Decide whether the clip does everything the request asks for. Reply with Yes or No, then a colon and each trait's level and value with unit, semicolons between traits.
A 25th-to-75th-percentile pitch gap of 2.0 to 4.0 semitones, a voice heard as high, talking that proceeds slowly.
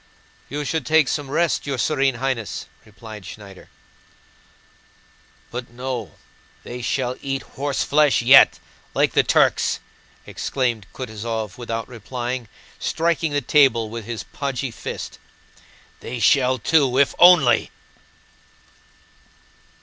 No: average, 3.4 semitones; low, 130 Hz; slow, 110 wpm